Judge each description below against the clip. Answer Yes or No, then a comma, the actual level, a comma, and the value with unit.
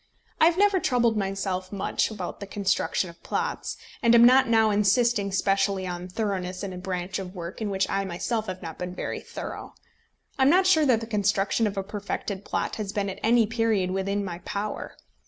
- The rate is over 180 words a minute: Yes, fast, 205 wpm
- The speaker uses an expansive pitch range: No, average, 3.2 semitones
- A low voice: No, high, 200 Hz